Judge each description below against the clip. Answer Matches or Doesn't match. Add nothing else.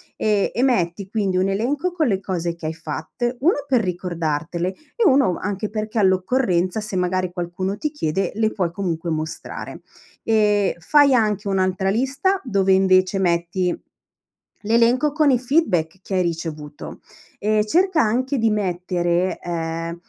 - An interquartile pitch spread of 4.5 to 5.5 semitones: Matches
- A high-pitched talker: Matches